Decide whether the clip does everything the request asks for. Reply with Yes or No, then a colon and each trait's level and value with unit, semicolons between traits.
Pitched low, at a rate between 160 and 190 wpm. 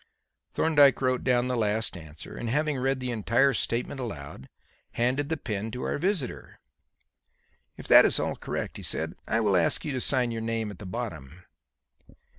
Yes: low, 120 Hz; average, 180 wpm